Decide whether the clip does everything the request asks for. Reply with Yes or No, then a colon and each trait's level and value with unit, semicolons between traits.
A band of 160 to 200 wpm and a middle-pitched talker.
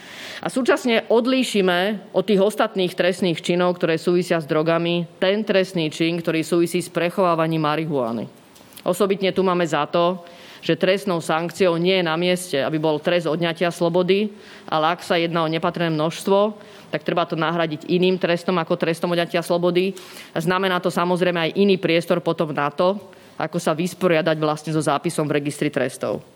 Yes: fast, 165 wpm; medium, 175 Hz